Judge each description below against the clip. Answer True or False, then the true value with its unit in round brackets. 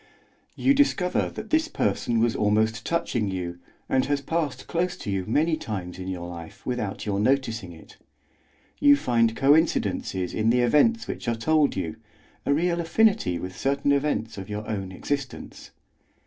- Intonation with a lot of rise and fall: True (8.0 semitones)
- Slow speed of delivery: False (160 wpm)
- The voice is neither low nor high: False (120 Hz)